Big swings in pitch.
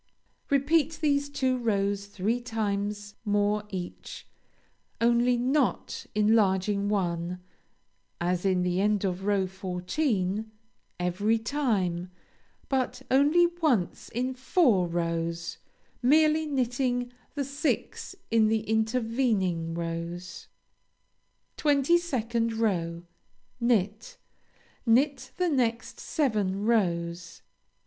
Yes: wide, 5.7 semitones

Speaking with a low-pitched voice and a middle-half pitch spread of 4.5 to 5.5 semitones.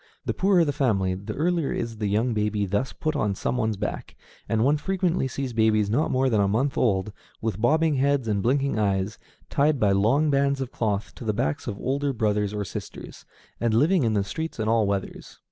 Yes: low, 115 Hz; average, 5.1 semitones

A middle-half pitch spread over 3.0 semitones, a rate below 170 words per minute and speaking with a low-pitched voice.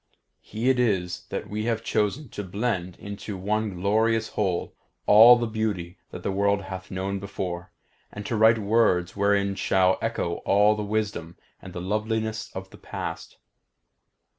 No: average, 2.7 semitones; average, 160 wpm; low, 100 Hz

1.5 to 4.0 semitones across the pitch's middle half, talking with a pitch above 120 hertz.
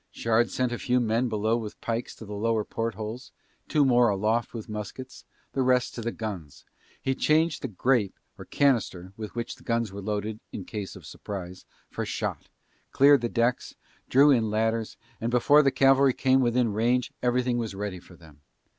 No: average, 3.1 semitones; low, 115 Hz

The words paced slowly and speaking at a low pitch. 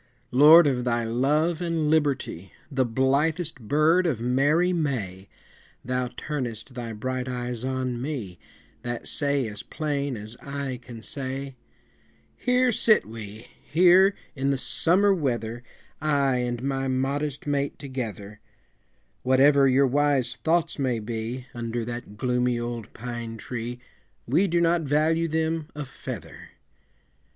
Yes: slow, 130 wpm; low, 130 Hz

